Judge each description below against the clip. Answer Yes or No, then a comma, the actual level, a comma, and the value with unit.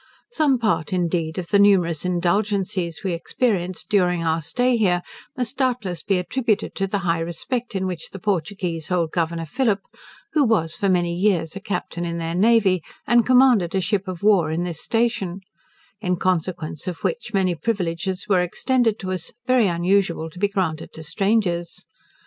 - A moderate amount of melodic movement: Yes, average, 3.5 semitones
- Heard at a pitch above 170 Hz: Yes, medium, 185 Hz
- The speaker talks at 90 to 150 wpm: No, average, 170 wpm